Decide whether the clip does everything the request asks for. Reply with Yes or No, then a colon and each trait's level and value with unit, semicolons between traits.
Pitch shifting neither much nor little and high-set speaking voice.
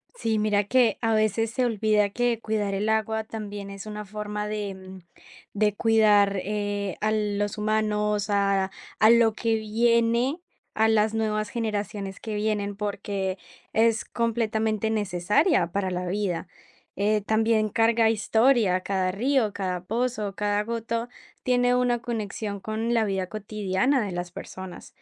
No: narrow, 1.9 semitones; high, 215 Hz